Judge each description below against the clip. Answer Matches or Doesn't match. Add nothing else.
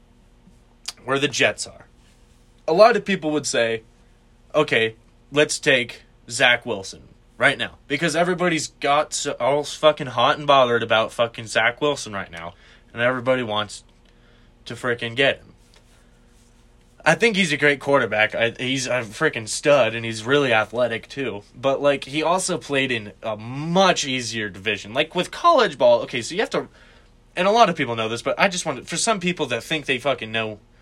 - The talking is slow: Doesn't match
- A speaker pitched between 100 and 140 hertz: Matches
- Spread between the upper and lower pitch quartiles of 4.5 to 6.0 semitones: Matches